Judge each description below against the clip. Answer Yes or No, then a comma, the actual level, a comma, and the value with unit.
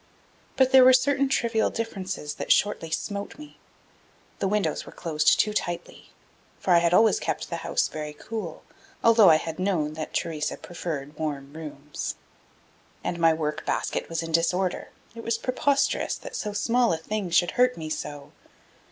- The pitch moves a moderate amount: No, wide, 6.3 semitones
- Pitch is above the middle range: No, medium, 175 Hz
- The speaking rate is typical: Yes, average, 170 wpm